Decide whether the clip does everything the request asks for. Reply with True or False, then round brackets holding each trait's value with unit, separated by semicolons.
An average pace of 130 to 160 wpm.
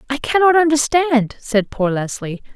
True (140 wpm)